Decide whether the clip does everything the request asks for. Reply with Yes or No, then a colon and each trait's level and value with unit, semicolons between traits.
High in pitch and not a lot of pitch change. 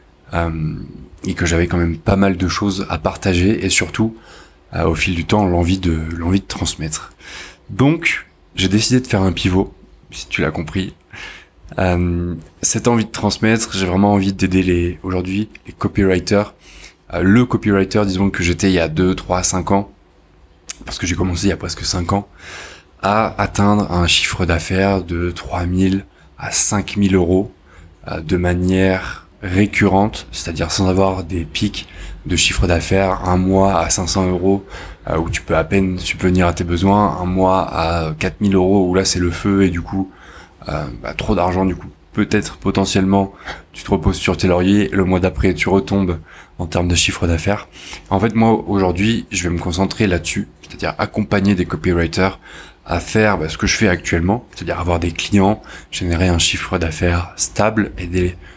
No: very low, 95 Hz; narrow, 2.3 semitones